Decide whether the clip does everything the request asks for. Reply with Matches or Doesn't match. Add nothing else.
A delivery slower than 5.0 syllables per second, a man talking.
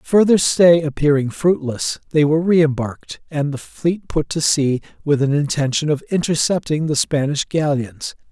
Matches